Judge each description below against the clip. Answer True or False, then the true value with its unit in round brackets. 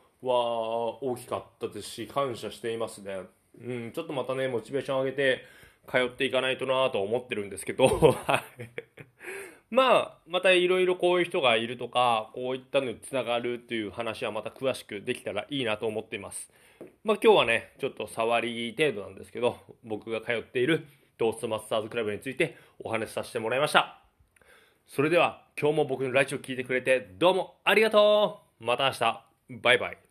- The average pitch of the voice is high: False (130 Hz)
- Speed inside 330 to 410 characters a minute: True (400 characters per minute)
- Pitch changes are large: False (4.4 semitones)